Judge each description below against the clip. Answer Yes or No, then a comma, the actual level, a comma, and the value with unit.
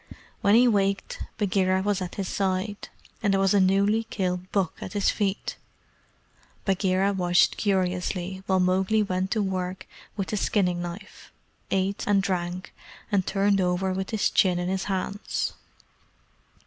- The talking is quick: No, average, 150 wpm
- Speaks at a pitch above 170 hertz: Yes, high, 190 Hz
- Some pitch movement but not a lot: No, narrow, 1.5 semitones